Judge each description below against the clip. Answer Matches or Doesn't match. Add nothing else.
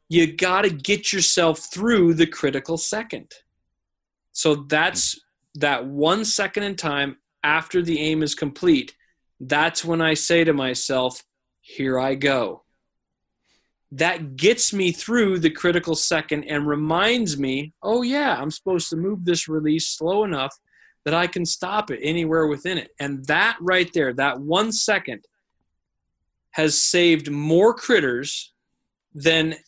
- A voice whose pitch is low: Doesn't match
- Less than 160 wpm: Matches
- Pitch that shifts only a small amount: Doesn't match